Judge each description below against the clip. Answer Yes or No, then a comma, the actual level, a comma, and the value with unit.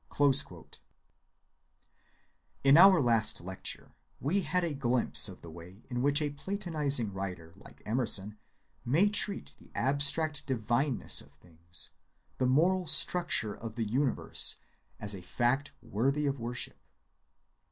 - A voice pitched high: No, low, 130 Hz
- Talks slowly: Yes, slow, 130 wpm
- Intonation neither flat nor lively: No, wide, 5.8 semitones